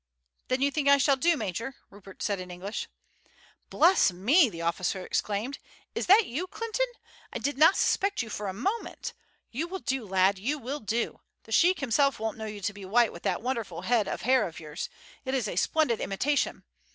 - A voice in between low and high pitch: No, high, 235 Hz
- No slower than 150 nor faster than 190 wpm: No, average, 200 wpm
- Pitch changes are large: Yes, wide, 6.3 semitones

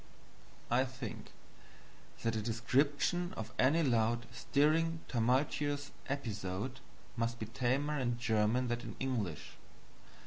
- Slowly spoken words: Yes, slow, 110 wpm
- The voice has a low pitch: Yes, low, 125 Hz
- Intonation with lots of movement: No, average, 3.7 semitones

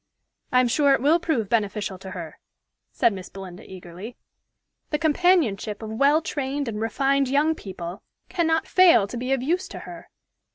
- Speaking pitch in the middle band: No, very high, 250 Hz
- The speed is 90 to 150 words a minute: No, average, 170 wpm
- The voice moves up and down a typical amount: No, wide, 6.9 semitones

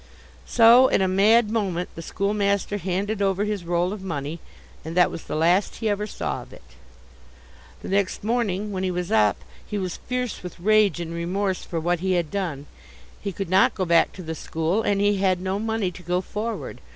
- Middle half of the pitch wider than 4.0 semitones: No, average, 2.9 semitones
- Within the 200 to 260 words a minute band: Yes, fast, 205 wpm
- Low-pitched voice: No, high, 190 Hz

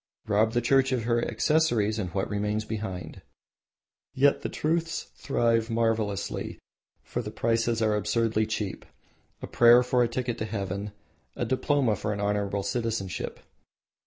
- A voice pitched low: Yes, low, 115 Hz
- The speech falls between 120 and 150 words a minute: Yes, average, 145 wpm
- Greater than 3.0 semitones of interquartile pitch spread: No, average, 2.7 semitones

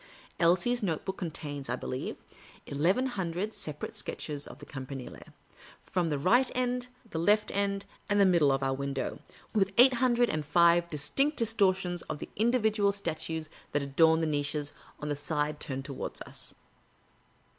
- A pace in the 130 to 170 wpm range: Yes, average, 160 wpm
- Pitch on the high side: No, medium, 170 Hz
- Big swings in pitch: Yes, wide, 5.9 semitones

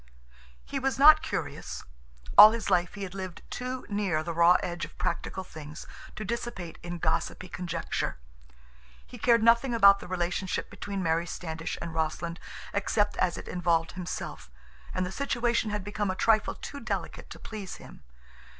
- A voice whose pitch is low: No, medium, 185 Hz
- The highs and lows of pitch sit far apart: No, average, 4.1 semitones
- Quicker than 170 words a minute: No, average, 165 wpm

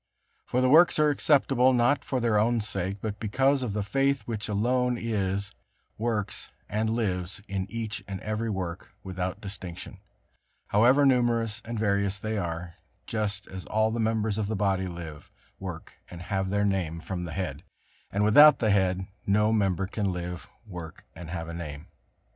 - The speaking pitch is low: Yes, low, 105 Hz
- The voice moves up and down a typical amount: Yes, average, 3.5 semitones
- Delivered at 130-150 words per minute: No, average, 170 wpm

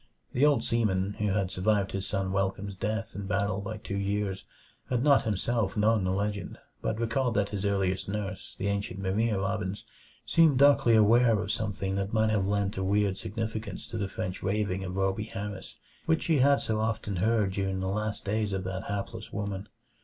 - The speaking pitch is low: Yes, low, 100 Hz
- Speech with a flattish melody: Yes, narrow, 2.2 semitones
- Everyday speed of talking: Yes, average, 190 wpm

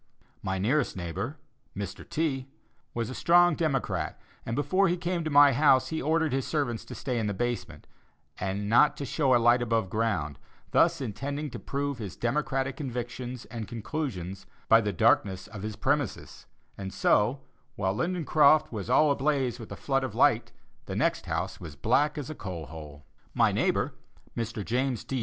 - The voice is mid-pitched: No, low, 125 Hz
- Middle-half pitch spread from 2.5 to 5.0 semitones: No, wide, 5.6 semitones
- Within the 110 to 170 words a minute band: No, average, 180 wpm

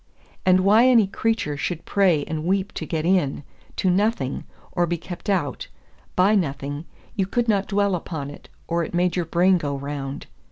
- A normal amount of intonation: Yes, average, 4.4 semitones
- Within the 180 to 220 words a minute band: Yes, average, 185 wpm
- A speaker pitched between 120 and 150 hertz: No, medium, 175 Hz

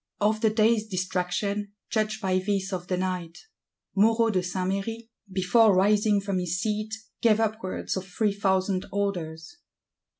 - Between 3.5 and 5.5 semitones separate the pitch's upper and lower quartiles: No, narrow, 2.6 semitones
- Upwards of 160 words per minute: No, average, 145 wpm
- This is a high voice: Yes, high, 200 Hz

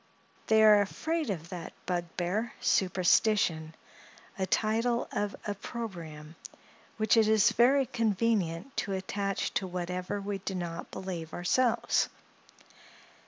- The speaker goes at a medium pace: No, slow, 110 wpm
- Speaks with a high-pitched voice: Yes, high, 195 Hz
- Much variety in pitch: No, average, 3.7 semitones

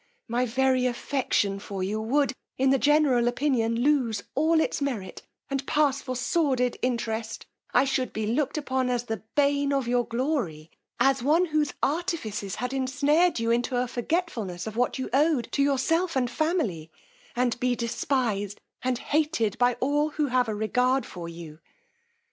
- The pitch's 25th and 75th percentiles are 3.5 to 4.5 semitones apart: Yes, average, 3.8 semitones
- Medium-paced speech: Yes, average, 165 wpm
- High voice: Yes, very high, 255 Hz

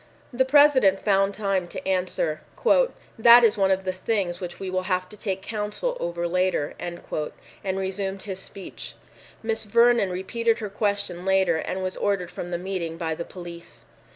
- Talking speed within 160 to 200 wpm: Yes, average, 170 wpm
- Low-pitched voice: No, high, 190 Hz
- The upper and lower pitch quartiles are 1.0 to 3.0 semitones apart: Yes, narrow, 2.4 semitones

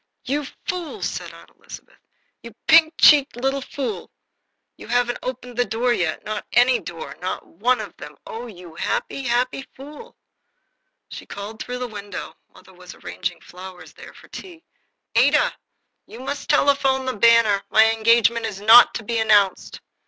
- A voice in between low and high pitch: No, high, 235 Hz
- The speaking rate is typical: Yes, average, 160 wpm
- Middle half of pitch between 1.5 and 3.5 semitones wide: No, average, 4.1 semitones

